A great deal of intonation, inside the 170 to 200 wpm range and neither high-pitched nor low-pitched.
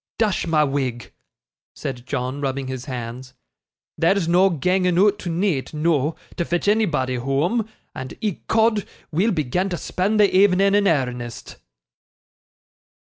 No: wide, 6.8 semitones; slow, 135 wpm; medium, 165 Hz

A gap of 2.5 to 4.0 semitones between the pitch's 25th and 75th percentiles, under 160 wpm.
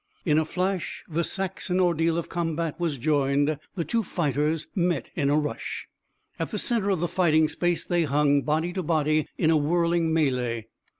No: average, 2.8 semitones; average, 180 wpm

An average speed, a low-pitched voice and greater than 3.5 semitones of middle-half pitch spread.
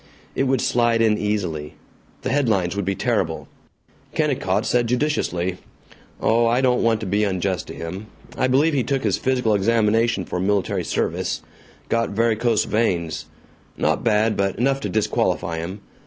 Yes: average, 155 wpm; low, 110 Hz; average, 4.1 semitones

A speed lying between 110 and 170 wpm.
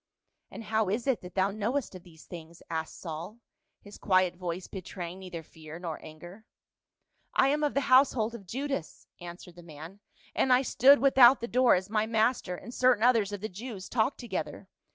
No: average, 195 wpm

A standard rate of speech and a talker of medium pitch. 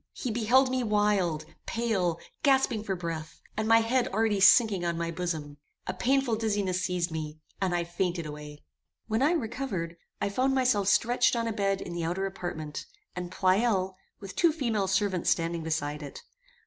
No: average, 175 wpm; high, 195 Hz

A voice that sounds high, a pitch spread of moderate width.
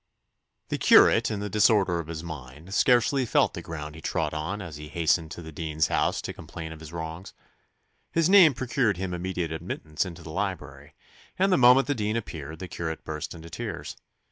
No: very low, 85 Hz; average, 4.9 semitones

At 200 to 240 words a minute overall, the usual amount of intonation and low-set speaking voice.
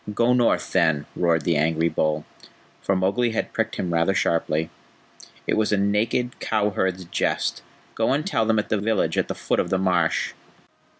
No: average, 185 wpm; average, 5.0 semitones; very low, 95 Hz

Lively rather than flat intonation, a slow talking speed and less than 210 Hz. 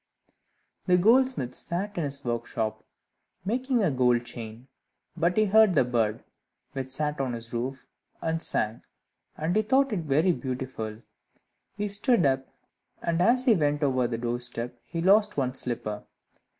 No: wide, 8.0 semitones; average, 155 wpm; medium, 140 Hz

